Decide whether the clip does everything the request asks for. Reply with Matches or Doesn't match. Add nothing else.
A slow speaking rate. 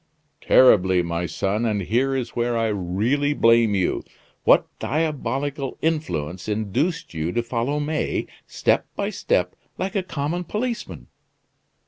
Matches